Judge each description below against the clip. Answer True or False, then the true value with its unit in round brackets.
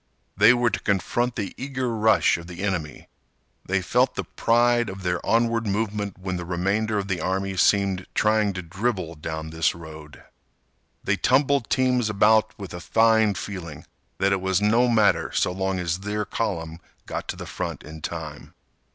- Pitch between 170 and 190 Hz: False (100 Hz)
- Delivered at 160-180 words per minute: True (175 wpm)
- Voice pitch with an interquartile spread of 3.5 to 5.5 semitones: True (3.9 semitones)